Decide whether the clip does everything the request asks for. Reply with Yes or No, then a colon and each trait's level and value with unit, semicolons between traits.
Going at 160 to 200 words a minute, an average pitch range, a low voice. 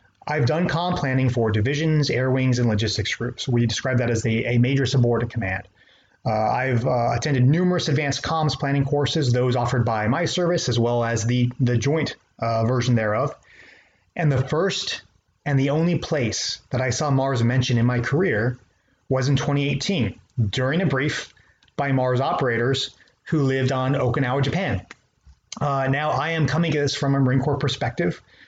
Yes: average, 175 wpm; average, 3.2 semitones; low, 130 Hz